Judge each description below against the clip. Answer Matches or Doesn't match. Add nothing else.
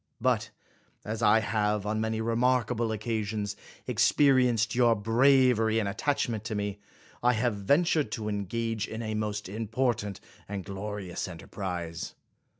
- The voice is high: Doesn't match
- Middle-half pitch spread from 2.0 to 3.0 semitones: Matches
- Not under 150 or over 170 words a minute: Doesn't match